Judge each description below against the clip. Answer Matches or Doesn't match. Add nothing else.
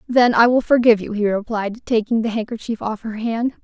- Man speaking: Doesn't match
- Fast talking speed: Matches